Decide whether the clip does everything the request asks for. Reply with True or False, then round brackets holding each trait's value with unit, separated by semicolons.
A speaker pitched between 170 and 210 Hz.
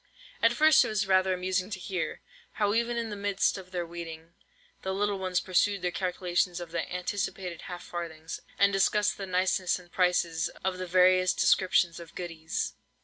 True (185 Hz)